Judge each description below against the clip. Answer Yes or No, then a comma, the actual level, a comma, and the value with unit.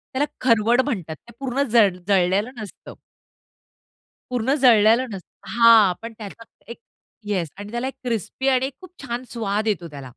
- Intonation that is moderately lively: Yes, average, 3.8 semitones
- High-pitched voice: Yes, high, 230 Hz